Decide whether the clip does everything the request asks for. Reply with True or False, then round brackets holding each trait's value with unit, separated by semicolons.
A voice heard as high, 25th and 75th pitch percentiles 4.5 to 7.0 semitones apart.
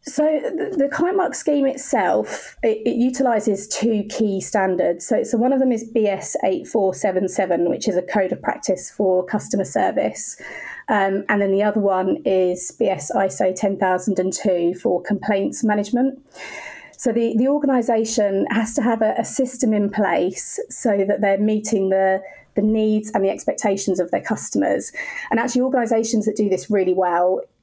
False (210 Hz; 3.9 semitones)